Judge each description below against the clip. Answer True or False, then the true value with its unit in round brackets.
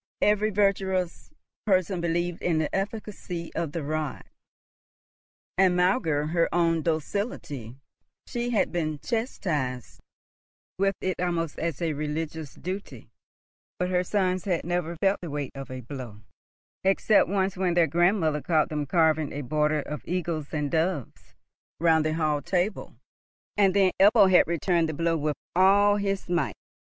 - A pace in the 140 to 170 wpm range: True (145 wpm)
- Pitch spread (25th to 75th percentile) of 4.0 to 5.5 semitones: False (3.6 semitones)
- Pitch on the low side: False (170 Hz)